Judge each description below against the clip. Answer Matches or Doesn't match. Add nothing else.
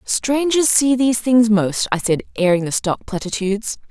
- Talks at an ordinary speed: Matches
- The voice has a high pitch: Matches